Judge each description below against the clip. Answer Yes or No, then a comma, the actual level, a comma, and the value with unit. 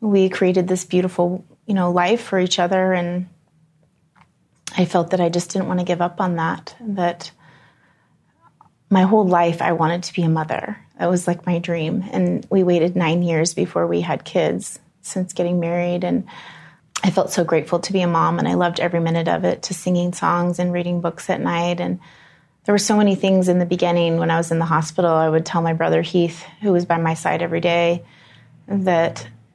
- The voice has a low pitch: No, medium, 175 Hz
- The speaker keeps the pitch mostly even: Yes, narrow, 1.7 semitones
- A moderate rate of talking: No, fast, 210 wpm